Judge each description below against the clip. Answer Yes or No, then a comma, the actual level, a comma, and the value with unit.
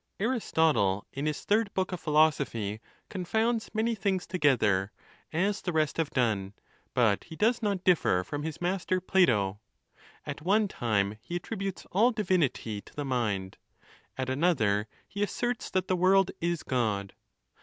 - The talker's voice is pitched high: No, medium, 160 Hz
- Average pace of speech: Yes, average, 155 wpm